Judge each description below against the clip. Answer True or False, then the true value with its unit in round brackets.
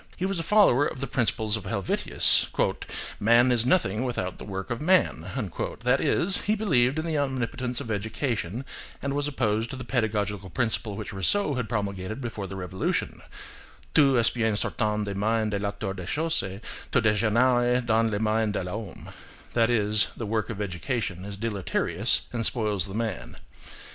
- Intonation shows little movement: False (3.7 semitones)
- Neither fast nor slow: True (170 wpm)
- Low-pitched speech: True (110 Hz)